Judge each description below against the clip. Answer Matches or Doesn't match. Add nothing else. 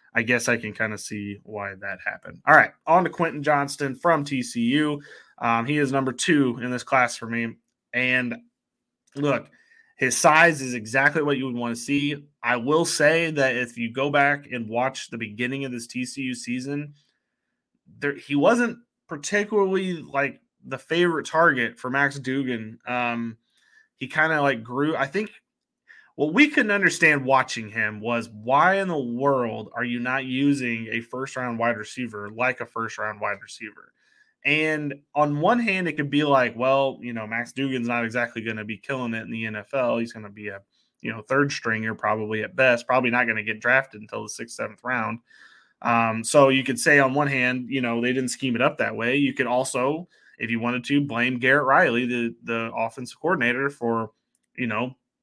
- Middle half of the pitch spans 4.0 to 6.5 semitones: Doesn't match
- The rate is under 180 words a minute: Doesn't match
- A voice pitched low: Matches